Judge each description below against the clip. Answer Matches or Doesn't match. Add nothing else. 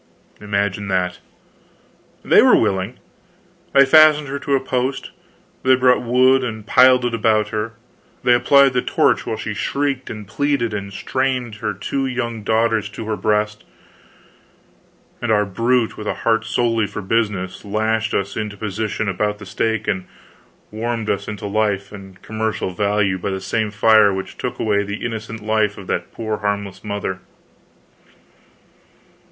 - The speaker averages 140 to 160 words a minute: Matches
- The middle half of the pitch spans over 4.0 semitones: Doesn't match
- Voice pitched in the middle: Doesn't match